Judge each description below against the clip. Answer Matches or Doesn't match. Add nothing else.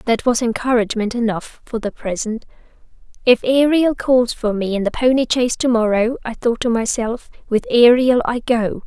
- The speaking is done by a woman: Matches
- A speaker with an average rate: Matches